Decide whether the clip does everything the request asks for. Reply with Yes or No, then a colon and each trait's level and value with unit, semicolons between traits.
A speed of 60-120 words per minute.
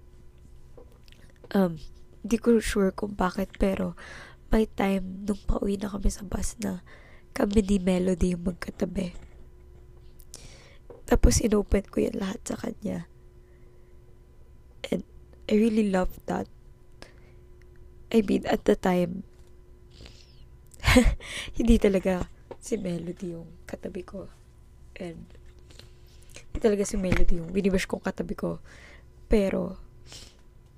Yes: slow, 110 wpm